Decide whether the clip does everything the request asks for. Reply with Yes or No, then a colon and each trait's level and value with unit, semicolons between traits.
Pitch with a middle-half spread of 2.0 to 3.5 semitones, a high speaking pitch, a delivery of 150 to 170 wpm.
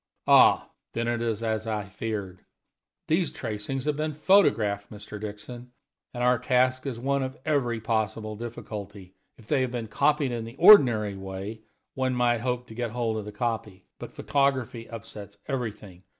No: average, 3.2 semitones; low, 115 Hz; average, 165 wpm